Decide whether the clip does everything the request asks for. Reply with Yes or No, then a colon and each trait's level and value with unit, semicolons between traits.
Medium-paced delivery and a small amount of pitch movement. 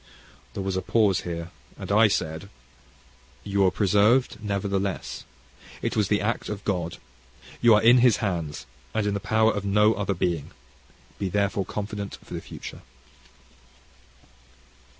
Yes: average, 150 wpm; narrow, 1.9 semitones